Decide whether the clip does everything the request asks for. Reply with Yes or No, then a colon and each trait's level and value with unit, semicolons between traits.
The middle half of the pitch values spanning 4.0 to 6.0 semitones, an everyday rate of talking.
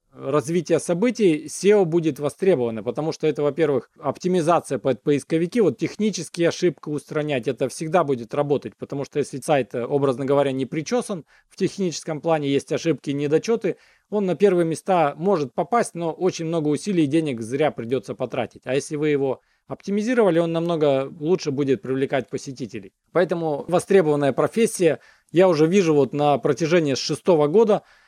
Yes: average, 4.3 semitones; average, 150 wpm